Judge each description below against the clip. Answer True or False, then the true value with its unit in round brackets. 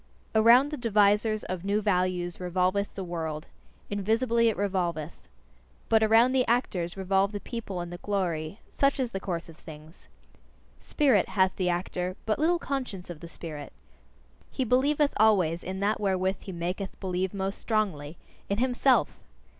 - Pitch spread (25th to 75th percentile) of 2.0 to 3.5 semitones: False (4.0 semitones)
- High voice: True (195 Hz)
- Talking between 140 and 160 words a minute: True (155 wpm)